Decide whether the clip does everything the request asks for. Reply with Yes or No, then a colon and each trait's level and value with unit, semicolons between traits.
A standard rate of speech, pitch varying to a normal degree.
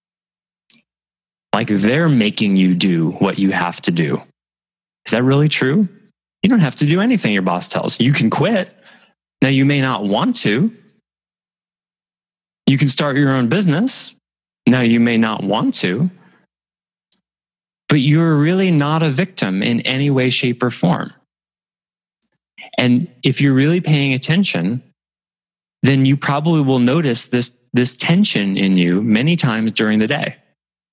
No: average, 150 wpm; wide, 6.9 semitones